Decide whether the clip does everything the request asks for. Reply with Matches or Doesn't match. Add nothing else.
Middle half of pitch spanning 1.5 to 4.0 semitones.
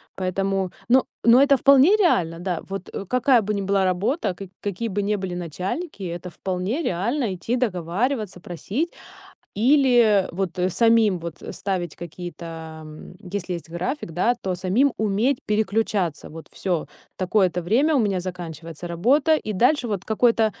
Doesn't match